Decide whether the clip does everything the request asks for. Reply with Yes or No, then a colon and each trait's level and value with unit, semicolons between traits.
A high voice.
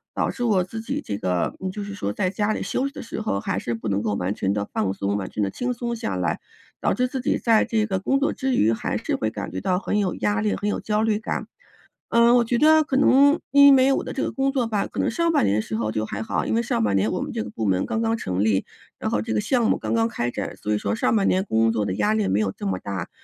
No: medium, 180 Hz